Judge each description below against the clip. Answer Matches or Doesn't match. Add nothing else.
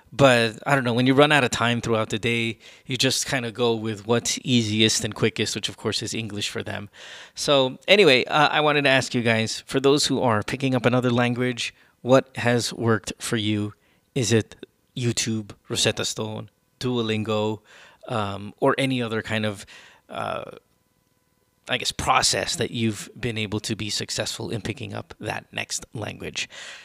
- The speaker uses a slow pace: Doesn't match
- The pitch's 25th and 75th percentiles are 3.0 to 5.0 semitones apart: Doesn't match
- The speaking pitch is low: Matches